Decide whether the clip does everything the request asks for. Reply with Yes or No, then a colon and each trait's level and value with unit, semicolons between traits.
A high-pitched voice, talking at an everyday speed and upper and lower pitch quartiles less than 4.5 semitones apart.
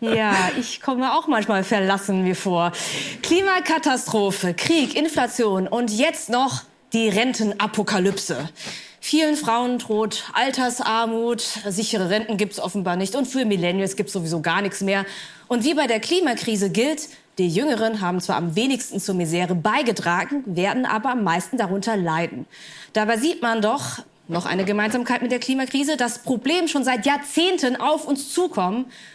No: high, 225 Hz; average, 150 wpm; average, 4.9 semitones